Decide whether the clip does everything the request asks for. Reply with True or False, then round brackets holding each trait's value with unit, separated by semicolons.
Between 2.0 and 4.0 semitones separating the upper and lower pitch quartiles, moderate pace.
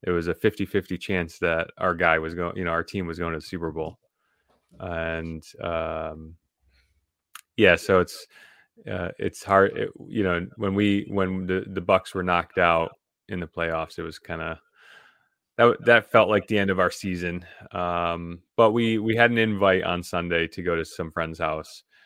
True (3.0 semitones; 195 wpm)